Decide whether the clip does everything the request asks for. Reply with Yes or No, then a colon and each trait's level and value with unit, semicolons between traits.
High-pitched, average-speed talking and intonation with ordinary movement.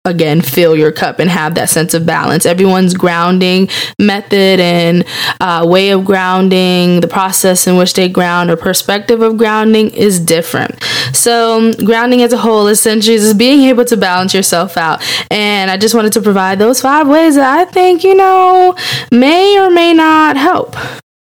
Yes: high, 195 Hz; average, 175 wpm; average, 4.7 semitones